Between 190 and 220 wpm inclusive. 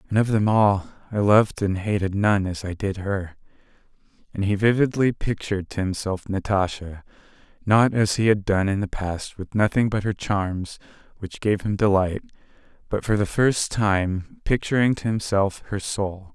No: average, 170 wpm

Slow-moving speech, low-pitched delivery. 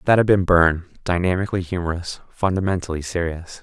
Yes: slow, 130 wpm; very low, 90 Hz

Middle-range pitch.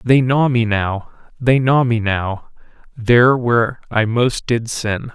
No: low, 120 Hz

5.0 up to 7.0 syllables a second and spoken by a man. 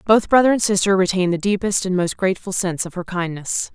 No: 6.4 syllables/s; female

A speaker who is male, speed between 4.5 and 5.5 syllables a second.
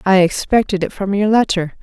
No: female; 5.4 syllables/s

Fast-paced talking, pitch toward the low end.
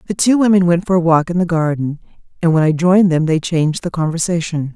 No: fast, 240 wpm; medium, 170 Hz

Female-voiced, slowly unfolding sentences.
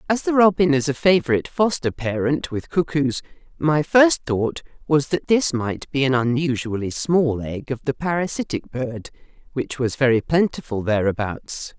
No: female; average, 160 wpm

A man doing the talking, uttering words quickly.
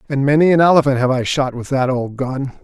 Yes: male; fast, 250 wpm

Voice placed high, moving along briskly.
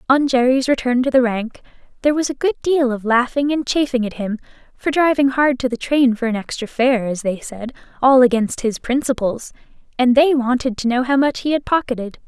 Yes: very high, 255 Hz; fast, 215 wpm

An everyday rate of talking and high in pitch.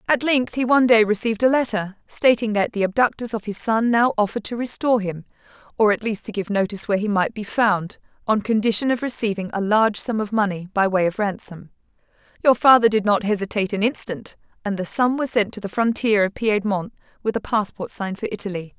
No: fast, 215 wpm; high, 215 Hz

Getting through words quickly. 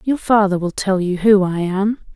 Yes: fast, 225 wpm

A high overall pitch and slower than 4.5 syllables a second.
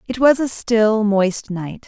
Yes: high, 220 Hz; 3.5 syllables/s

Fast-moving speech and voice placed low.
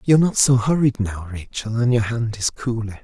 Yes: fast, 215 wpm; low, 115 Hz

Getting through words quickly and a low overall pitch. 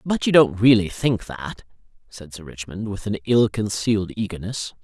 No: average, 175 wpm; low, 100 Hz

